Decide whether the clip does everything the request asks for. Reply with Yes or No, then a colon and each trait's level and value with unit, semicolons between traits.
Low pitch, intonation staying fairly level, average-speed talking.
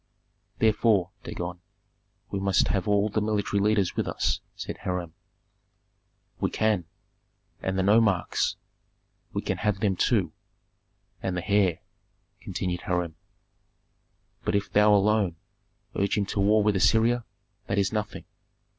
No: low, 100 Hz; narrow, 2.3 semitones; slow, 130 wpm